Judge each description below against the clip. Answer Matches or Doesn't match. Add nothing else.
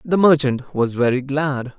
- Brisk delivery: Doesn't match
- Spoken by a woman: Doesn't match